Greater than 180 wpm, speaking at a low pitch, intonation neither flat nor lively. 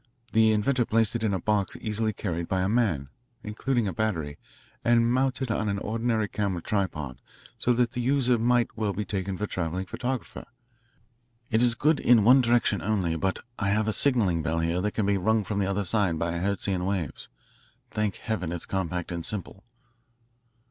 Yes: average, 190 wpm; low, 105 Hz; average, 3.8 semitones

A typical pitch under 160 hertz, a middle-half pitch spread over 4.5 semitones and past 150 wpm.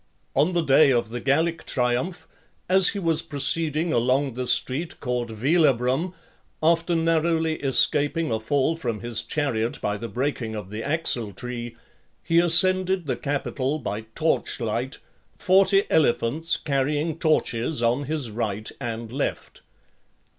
No: medium, 140 Hz; wide, 5.4 semitones; average, 140 wpm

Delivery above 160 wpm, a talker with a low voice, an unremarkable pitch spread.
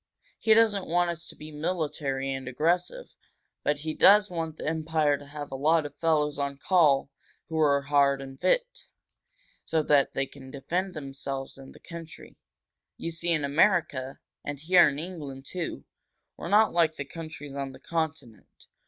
No: average, 170 wpm; medium, 155 Hz; average, 3.3 semitones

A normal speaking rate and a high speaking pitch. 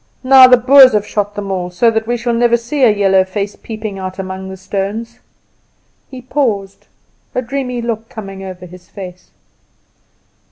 Yes: average, 170 wpm; high, 210 Hz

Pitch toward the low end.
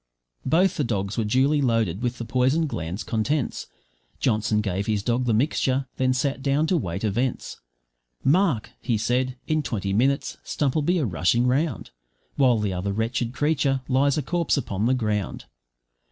Yes: low, 125 Hz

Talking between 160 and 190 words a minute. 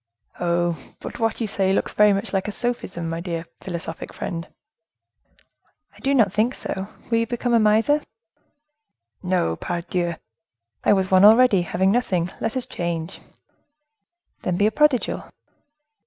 No: average, 145 wpm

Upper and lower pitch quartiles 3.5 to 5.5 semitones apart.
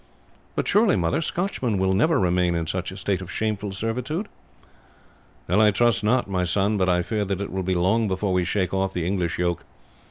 No: average, 3.1 semitones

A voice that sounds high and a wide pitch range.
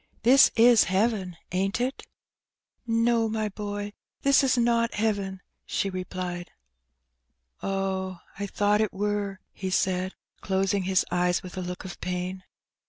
No: high, 195 Hz; average, 3.0 semitones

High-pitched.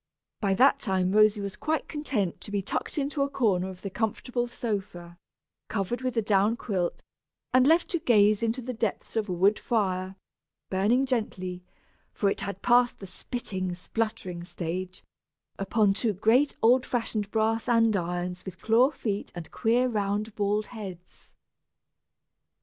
Yes: high, 210 Hz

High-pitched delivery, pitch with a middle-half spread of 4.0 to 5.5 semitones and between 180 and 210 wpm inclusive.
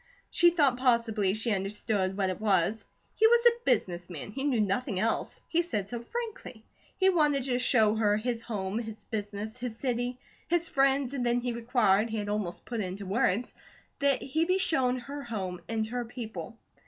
Yes: high, 235 Hz; average, 4.3 semitones; average, 190 wpm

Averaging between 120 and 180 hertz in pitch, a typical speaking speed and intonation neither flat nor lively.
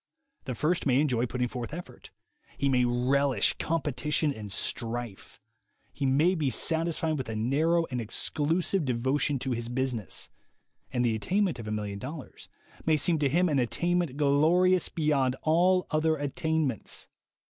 Yes: medium, 140 Hz; average, 150 wpm; average, 4.6 semitones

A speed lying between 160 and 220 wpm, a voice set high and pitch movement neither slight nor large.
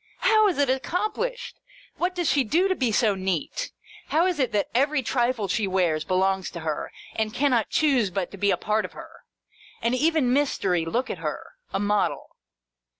No: average, 190 wpm; high, 245 Hz; wide, 7.7 semitones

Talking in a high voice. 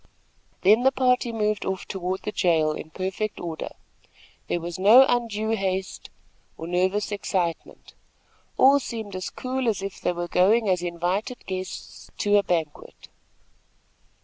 Yes: high, 195 Hz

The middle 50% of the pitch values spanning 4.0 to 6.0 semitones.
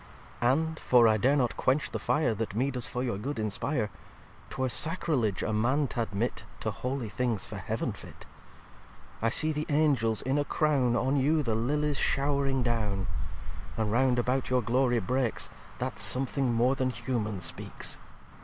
No: average, 3.5 semitones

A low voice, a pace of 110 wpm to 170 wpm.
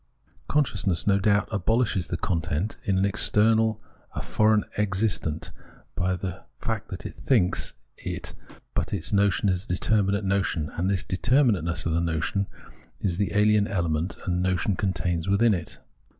Yes: very low, 95 Hz; average, 150 wpm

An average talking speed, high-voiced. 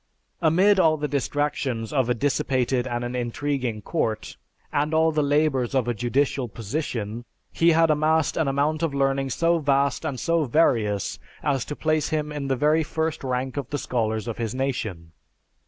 No: average, 175 wpm; medium, 140 Hz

